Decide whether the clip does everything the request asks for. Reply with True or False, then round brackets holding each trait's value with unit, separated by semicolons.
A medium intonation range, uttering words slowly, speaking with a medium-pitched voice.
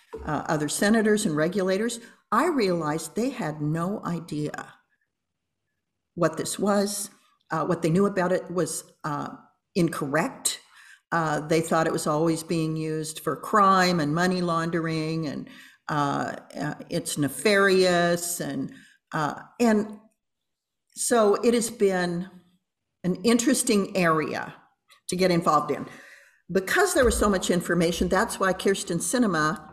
True (4.0 semitones; 130 wpm; 180 Hz)